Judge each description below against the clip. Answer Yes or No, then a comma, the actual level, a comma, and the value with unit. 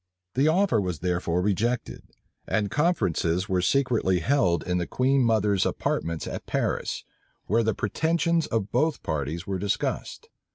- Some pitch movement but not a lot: No, wide, 7.2 semitones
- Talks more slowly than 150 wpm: Yes, average, 140 wpm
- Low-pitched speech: Yes, low, 105 Hz